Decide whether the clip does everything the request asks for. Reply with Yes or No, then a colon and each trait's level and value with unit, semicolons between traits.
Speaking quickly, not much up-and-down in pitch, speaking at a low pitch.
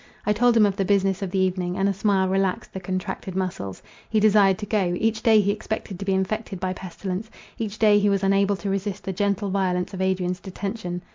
No: fast, 225 wpm; narrow, 1.8 semitones; high, 195 Hz